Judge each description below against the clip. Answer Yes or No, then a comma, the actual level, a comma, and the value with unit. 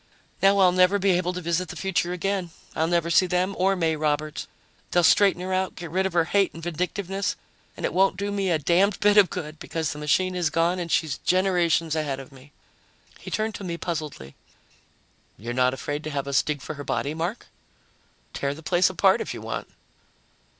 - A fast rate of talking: Yes, fast, 210 wpm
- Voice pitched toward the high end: No, medium, 175 Hz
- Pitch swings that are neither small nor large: Yes, average, 3.4 semitones